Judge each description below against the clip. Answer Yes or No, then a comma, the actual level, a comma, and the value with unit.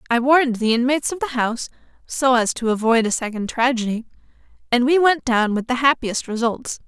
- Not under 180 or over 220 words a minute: Yes, average, 190 wpm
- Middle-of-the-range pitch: No, high, 245 Hz